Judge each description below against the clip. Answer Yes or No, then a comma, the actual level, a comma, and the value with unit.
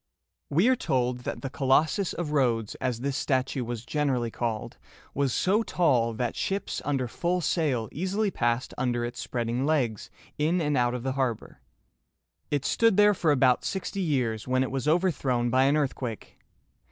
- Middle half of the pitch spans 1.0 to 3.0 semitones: No, average, 4.5 semitones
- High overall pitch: No, low, 135 Hz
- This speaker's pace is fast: No, average, 175 wpm